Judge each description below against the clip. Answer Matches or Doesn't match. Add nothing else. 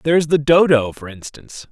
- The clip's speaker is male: Matches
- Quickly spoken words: Matches